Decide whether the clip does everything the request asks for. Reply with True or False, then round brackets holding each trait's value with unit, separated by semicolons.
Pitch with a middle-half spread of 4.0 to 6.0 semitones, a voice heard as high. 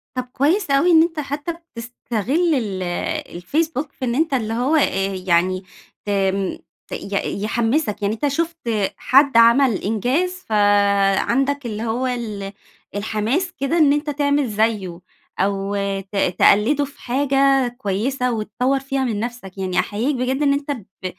True (5.6 semitones; 245 Hz)